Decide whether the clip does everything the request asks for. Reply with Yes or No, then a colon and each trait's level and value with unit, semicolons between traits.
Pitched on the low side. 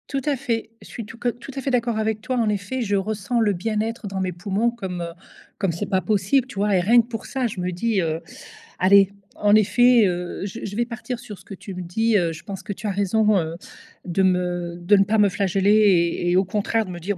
No: high, 205 Hz